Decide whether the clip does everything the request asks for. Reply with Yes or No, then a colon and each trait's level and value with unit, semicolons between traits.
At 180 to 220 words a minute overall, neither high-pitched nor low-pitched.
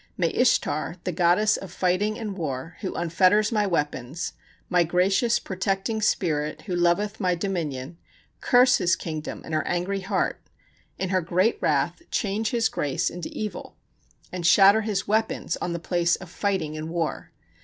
No: average, 160 wpm; medium, 180 Hz